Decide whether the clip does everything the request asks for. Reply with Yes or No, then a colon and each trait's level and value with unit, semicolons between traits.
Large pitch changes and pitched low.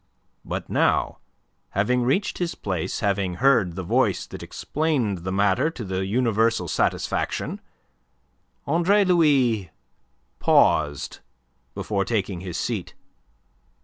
Yes: wide, 6.5 semitones; low, 110 Hz